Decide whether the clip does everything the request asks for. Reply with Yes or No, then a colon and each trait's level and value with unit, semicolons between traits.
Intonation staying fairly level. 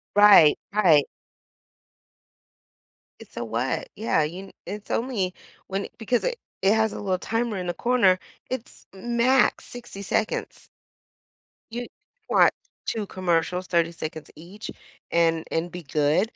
No: average, 4.9 semitones